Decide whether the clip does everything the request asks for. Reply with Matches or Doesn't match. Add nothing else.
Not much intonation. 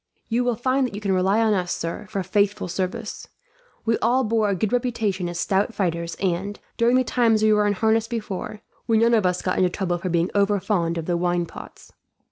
Doesn't match